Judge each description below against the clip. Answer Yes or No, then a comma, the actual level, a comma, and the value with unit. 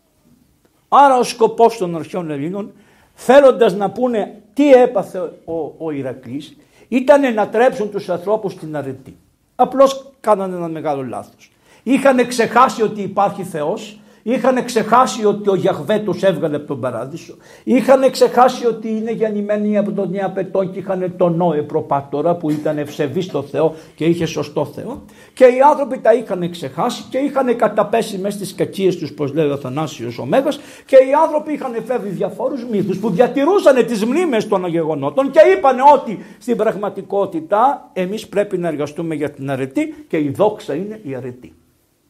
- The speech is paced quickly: No, average, 155 wpm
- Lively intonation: Yes, wide, 6.7 semitones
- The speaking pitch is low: No, high, 205 Hz